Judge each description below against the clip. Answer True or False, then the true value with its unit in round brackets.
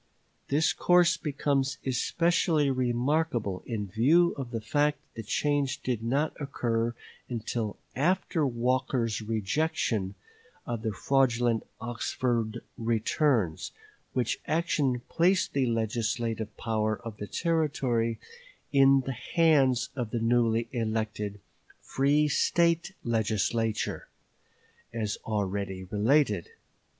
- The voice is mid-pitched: False (120 Hz)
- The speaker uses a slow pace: True (105 wpm)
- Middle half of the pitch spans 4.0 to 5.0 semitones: True (4.3 semitones)